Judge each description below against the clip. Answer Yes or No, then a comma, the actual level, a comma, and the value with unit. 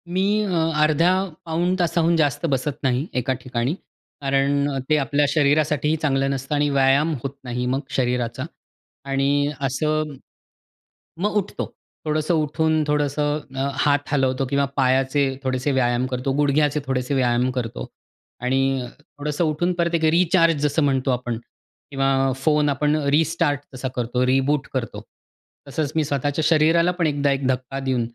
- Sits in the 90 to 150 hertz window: Yes, medium, 140 Hz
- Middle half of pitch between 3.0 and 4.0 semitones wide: No, narrow, 2.5 semitones